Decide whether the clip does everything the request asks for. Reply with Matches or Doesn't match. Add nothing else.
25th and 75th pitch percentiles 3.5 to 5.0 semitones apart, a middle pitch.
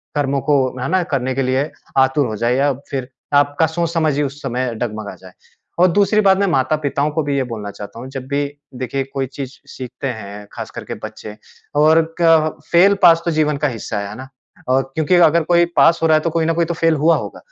Matches